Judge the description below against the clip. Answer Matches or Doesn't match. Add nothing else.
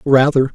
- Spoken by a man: Matches